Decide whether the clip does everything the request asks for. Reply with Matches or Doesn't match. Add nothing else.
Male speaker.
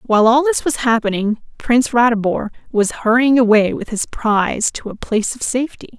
Doesn't match